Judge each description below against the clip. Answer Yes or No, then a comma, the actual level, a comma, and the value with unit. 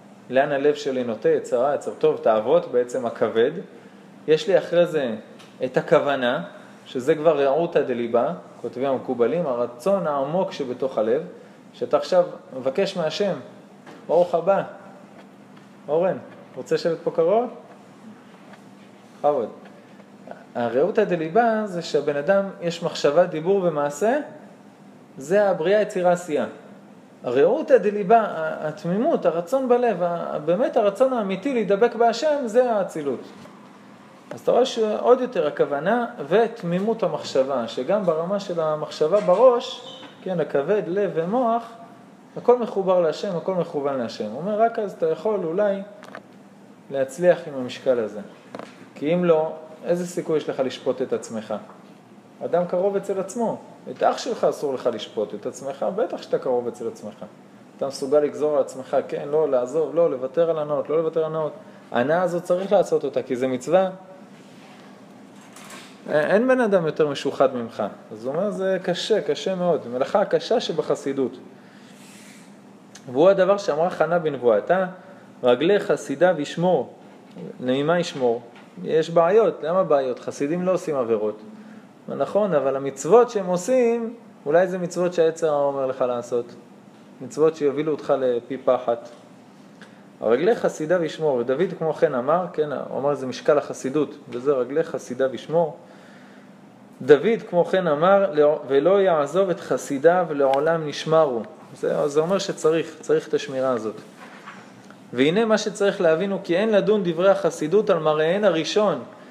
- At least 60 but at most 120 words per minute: No, average, 140 wpm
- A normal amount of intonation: No, wide, 6.3 semitones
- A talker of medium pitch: Yes, medium, 180 Hz